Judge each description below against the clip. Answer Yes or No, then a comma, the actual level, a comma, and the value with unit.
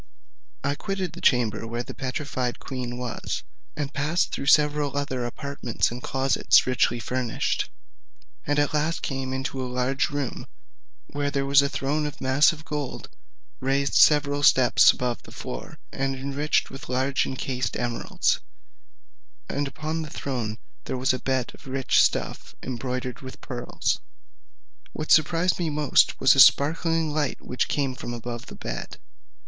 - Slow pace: No, average, 155 wpm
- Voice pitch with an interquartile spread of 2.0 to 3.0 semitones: Yes, narrow, 2.5 semitones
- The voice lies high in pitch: No, low, 135 Hz